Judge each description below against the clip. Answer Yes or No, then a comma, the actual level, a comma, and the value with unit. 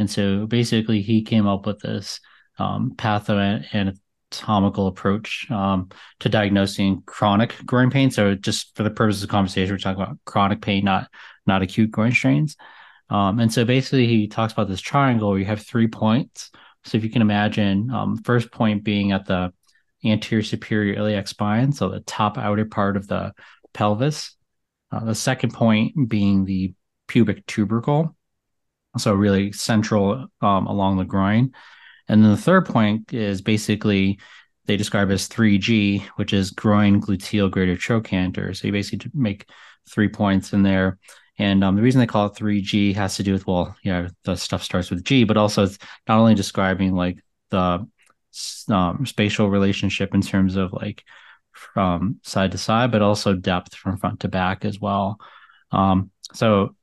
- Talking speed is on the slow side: No, average, 170 wpm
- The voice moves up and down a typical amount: No, narrow, 2.3 semitones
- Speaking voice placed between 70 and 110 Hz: Yes, low, 105 Hz